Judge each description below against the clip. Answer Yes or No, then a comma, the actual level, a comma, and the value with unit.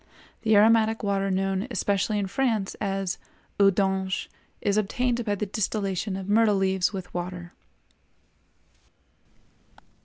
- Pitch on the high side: Yes, high, 200 Hz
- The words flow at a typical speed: No, slow, 120 wpm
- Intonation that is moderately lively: No, narrow, 2.0 semitones